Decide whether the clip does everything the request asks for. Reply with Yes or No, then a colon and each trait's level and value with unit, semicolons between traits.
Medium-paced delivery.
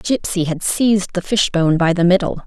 Yes: average, 195 wpm